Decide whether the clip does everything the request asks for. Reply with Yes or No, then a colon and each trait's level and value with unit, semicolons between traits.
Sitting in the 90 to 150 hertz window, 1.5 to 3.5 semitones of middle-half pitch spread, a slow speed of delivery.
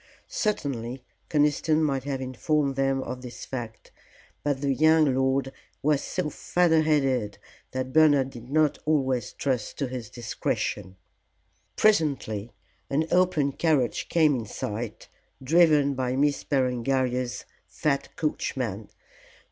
Yes: low, 135 Hz; average, 3.2 semitones; slow, 120 wpm